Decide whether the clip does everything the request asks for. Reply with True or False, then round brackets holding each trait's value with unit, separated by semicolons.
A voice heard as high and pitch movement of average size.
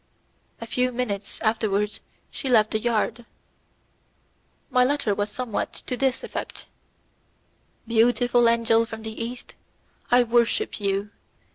False (230 Hz; 2.2 semitones)